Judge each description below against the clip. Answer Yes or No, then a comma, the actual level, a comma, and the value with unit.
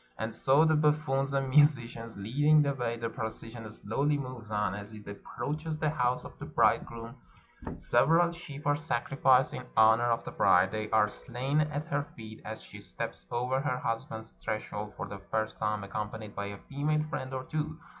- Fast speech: No, average, 185 wpm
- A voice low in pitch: Yes, low, 125 Hz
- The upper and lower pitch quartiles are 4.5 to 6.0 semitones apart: Yes, average, 4.8 semitones